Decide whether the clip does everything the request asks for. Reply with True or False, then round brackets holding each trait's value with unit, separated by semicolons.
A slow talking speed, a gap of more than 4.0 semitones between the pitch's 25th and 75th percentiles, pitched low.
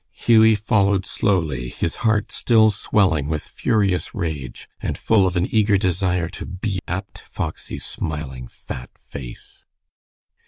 True (130 wpm; 5.1 semitones; 95 Hz)